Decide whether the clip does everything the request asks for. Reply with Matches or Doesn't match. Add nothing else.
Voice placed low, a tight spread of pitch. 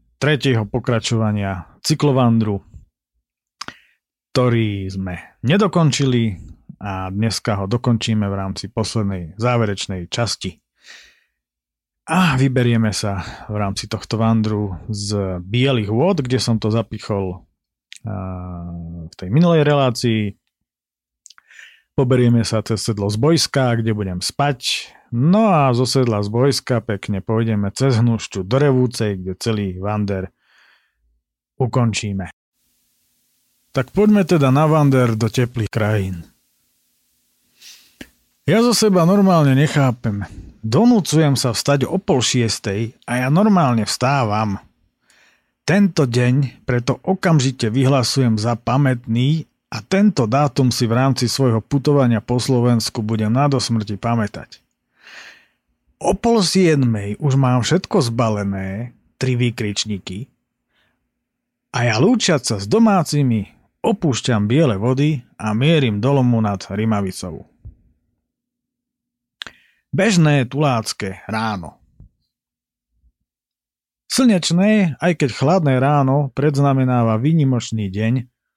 Doesn't match